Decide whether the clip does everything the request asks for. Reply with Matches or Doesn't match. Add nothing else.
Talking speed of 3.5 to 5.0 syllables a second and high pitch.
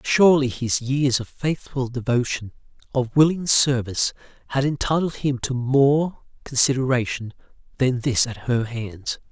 Doesn't match